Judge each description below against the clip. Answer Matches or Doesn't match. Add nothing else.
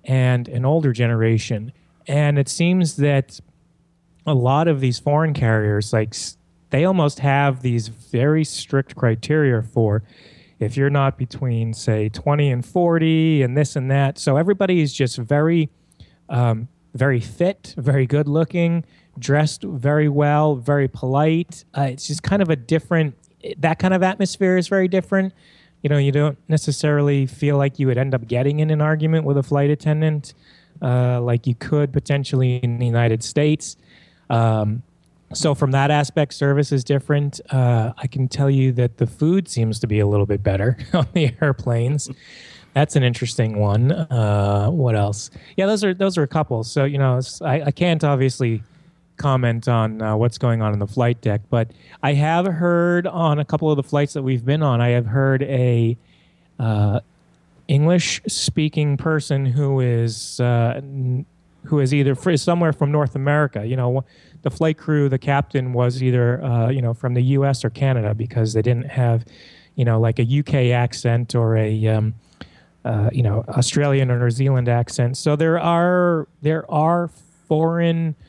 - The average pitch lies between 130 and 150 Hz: Matches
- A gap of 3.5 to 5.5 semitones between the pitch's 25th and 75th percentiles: Matches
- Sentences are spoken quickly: Doesn't match